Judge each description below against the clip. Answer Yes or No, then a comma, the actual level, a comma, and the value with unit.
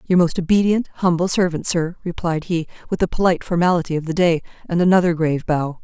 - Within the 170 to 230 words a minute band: Yes, average, 195 wpm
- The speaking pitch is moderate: Yes, medium, 170 Hz